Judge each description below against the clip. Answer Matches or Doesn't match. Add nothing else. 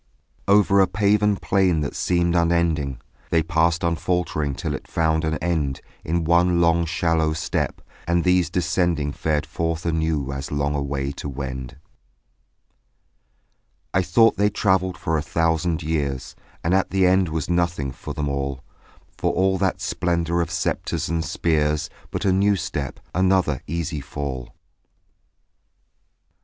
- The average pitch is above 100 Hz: Doesn't match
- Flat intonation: Doesn't match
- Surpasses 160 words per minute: Doesn't match